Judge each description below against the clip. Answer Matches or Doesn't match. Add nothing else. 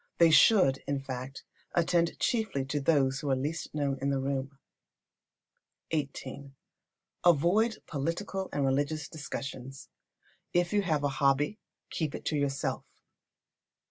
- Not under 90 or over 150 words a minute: Matches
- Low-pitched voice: Doesn't match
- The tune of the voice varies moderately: Matches